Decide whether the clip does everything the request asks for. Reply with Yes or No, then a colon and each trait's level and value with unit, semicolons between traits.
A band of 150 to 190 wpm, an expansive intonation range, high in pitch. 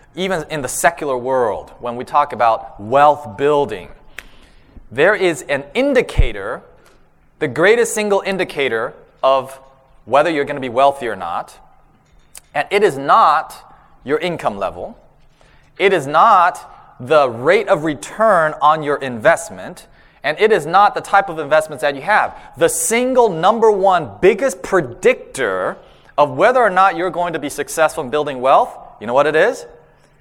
No: average, 155 wpm; wide, 6.2 semitones; medium, 155 Hz